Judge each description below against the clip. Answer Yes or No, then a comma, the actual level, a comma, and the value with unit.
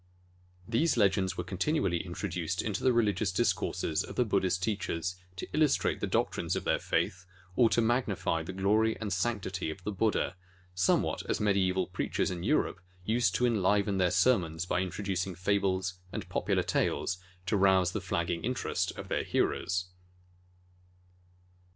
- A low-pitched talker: Yes, very low, 95 Hz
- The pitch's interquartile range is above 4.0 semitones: No, average, 3.2 semitones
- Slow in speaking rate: No, average, 155 wpm